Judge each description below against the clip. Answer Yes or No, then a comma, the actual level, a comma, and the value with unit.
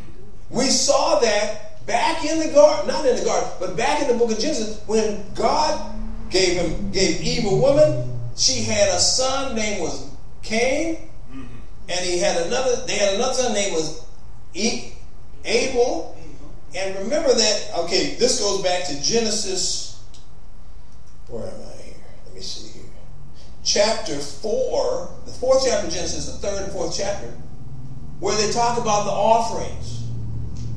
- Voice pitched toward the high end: Yes, high, 200 Hz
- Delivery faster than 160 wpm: No, average, 155 wpm